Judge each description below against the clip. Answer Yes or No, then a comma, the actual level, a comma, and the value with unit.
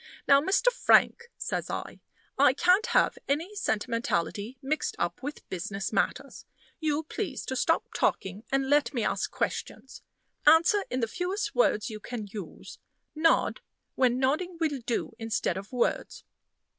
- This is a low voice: No, very high, 270 Hz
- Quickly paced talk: No, average, 145 wpm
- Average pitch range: No, wide, 6.6 semitones